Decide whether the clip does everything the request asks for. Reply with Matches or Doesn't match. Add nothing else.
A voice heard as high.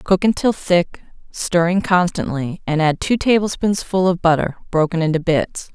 Doesn't match